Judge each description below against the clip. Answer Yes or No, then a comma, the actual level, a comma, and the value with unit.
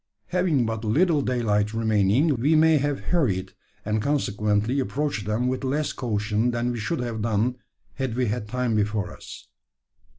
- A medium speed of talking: Yes, average, 160 wpm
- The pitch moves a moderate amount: Yes, average, 4.6 semitones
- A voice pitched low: Yes, low, 120 Hz